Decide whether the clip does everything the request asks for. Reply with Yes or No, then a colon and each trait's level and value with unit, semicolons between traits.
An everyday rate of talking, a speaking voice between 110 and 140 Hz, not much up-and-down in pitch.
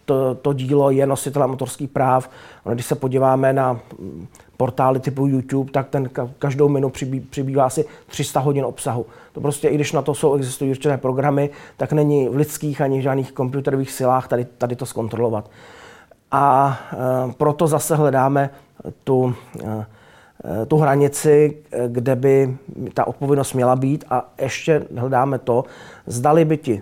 Yes: average, 150 wpm; low, 135 Hz; narrow, 2.2 semitones